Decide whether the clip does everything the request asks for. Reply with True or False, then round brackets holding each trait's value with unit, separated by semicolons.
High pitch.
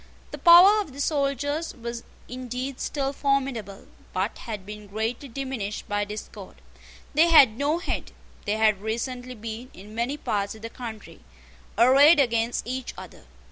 True (245 Hz)